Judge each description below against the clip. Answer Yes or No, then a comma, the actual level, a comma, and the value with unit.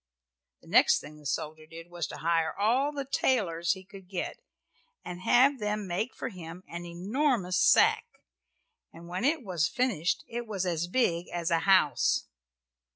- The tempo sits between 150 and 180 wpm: Yes, average, 165 wpm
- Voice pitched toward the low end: No, medium, 180 Hz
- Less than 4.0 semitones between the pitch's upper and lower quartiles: No, average, 5.1 semitones